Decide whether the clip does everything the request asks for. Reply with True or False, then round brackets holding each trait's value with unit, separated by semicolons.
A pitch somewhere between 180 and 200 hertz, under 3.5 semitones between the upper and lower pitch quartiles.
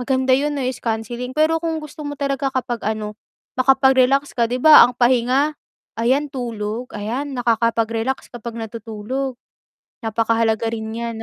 False (245 Hz; 3.0 semitones)